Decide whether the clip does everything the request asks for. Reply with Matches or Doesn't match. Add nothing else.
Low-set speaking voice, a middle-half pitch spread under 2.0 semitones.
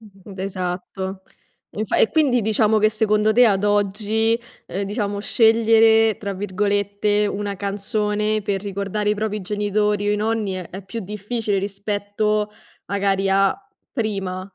Doesn't match